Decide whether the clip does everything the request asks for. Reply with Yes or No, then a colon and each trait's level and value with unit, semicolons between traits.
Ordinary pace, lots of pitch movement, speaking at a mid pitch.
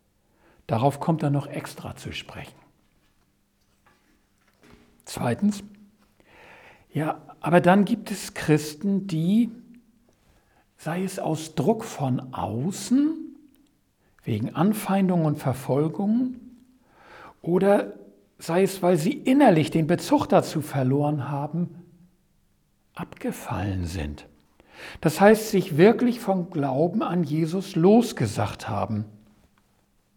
No: slow, 95 wpm; wide, 6.7 semitones; medium, 175 Hz